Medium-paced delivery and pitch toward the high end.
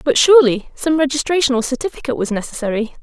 Yes: average, 160 wpm; very high, 270 Hz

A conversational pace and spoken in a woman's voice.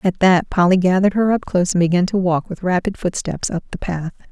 No: fast, 235 wpm; female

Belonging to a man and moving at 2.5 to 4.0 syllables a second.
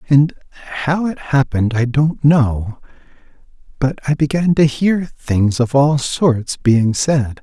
Yes: male; 3.7 syllables/s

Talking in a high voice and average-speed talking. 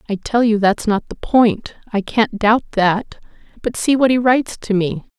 Yes: high, 220 Hz; average, 195 wpm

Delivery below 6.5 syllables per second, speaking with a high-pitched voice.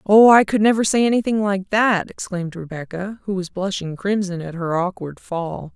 Yes: 5.0 syllables/s; high, 195 Hz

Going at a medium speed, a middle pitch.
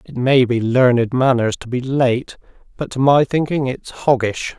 No: average, 185 wpm; low, 130 Hz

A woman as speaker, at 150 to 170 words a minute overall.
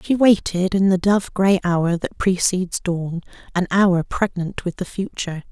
Yes: female; average, 165 wpm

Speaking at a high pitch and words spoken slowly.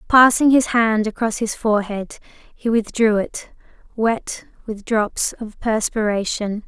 Yes: high, 220 Hz; slow, 125 wpm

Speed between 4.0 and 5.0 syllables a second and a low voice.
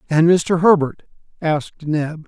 No: 4.1 syllables/s; medium, 160 Hz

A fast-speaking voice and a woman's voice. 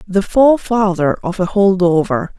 No: average, 150 wpm; female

